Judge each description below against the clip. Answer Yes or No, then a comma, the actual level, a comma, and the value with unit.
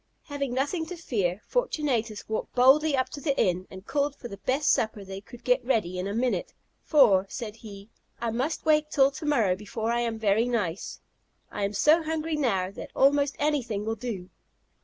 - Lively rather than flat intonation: Yes, wide, 5.8 semitones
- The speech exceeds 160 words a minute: Yes, average, 195 wpm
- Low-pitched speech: No, high, 240 Hz